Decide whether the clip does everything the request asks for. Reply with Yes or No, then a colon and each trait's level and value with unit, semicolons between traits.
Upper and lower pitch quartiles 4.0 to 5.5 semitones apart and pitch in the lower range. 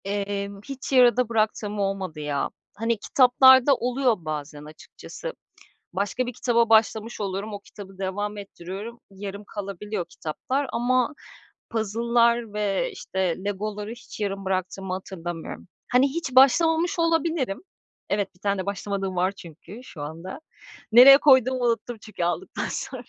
No: average, 4.3 semitones; high, 210 Hz